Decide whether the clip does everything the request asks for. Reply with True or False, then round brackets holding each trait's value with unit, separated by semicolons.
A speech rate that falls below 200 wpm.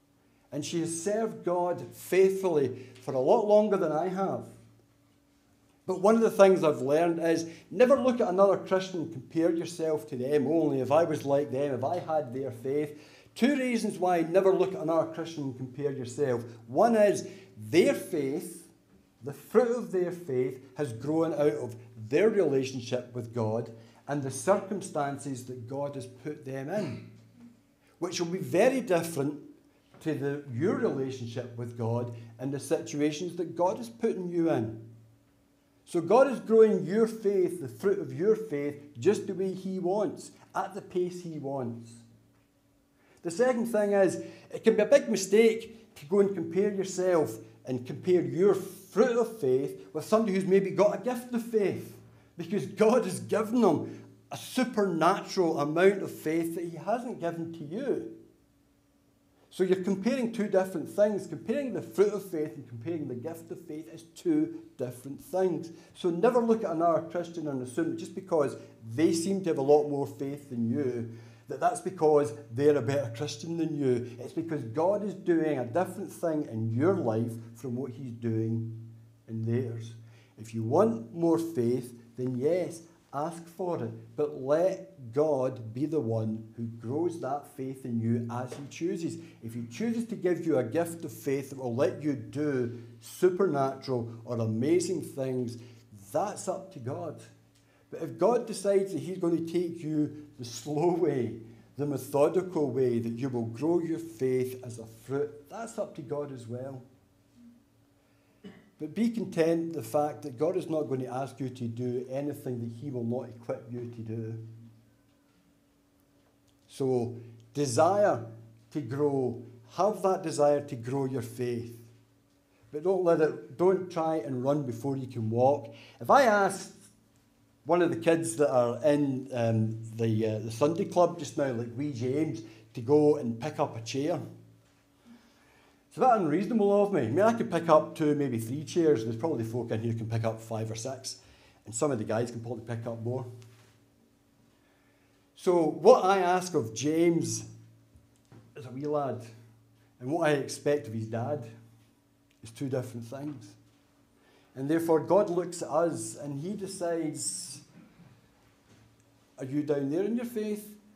True (175 wpm)